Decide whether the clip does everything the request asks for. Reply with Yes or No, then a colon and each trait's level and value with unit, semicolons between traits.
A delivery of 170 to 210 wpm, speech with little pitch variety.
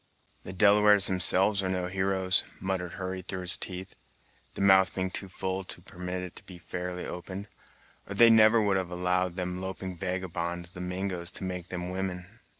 Yes: average, 180 wpm; narrow, 1.1 semitones